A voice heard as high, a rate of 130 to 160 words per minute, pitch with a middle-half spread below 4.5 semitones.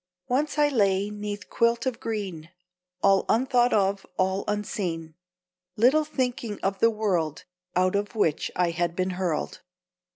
Yes: high, 205 Hz; average, 140 wpm; average, 4.0 semitones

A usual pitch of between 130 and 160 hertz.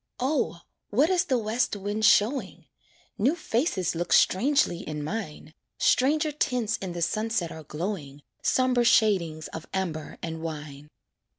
No: high, 205 Hz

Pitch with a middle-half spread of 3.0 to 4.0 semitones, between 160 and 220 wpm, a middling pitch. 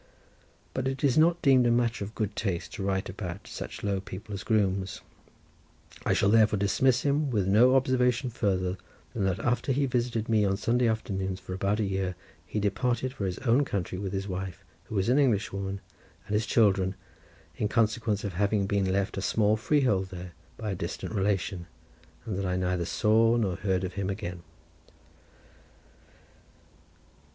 No: average, 3.5 semitones; average, 180 wpm; low, 105 Hz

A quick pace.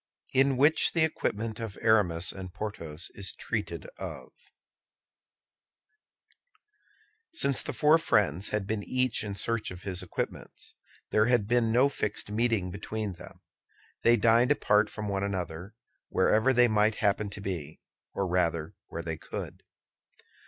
No: average, 140 wpm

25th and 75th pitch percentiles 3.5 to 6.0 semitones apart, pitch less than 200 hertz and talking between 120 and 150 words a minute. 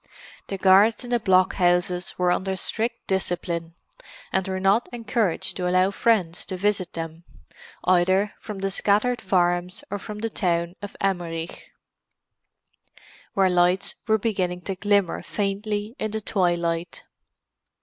No: narrow, 2.6 semitones; high, 190 Hz; slow, 135 wpm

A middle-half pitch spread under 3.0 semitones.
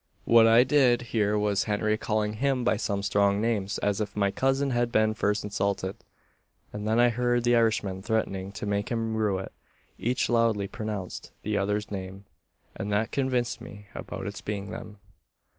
Yes: narrow, 2.5 semitones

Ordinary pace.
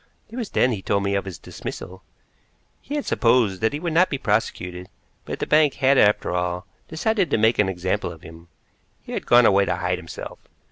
No: fast, 215 wpm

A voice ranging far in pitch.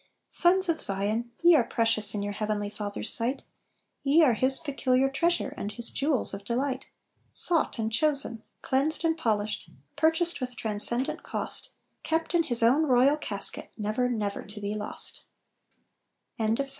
Yes: wide, 6.2 semitones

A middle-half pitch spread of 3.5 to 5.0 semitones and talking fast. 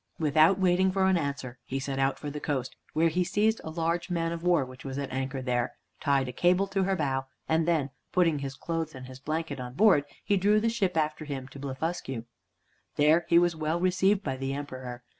Yes: average, 4.7 semitones; fast, 220 wpm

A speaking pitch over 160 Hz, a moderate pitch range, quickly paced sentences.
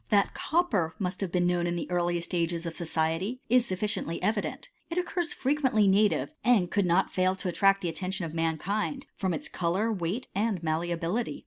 Yes: medium, 185 Hz; average, 4.1 semitones; fast, 210 wpm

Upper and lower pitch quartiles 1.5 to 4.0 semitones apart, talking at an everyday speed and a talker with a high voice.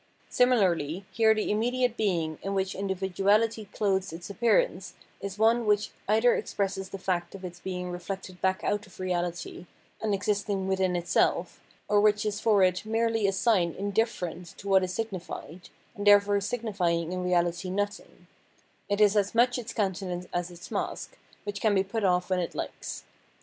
Yes: average, 2.8 semitones; average, 170 wpm; high, 195 Hz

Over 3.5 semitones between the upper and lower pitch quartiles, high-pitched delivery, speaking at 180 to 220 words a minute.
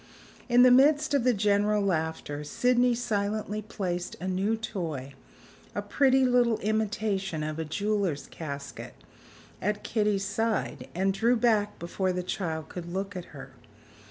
No: average, 4.3 semitones; high, 205 Hz; average, 145 wpm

